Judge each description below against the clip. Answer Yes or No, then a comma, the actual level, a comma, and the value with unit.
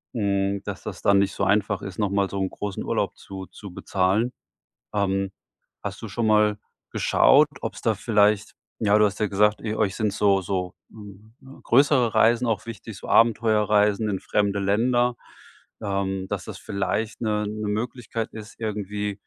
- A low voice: Yes, low, 105 Hz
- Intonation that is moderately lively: No, narrow, 2.0 semitones